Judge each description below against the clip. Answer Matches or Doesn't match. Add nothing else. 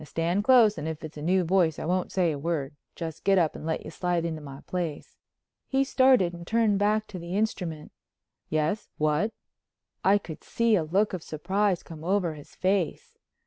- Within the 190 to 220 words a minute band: Matches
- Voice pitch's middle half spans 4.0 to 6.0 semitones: Matches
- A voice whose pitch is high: Doesn't match